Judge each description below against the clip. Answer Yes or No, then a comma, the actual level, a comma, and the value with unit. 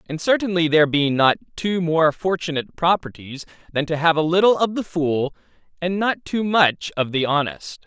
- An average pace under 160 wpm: No, average, 185 wpm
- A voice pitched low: No, medium, 160 Hz